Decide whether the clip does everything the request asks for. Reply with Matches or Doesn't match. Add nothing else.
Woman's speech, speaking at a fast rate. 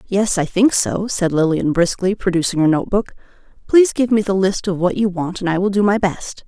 Matches